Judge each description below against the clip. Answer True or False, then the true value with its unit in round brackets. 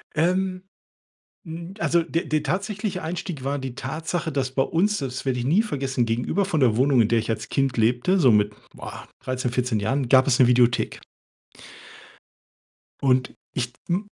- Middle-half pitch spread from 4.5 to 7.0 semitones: True (5.6 semitones)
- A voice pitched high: False (135 Hz)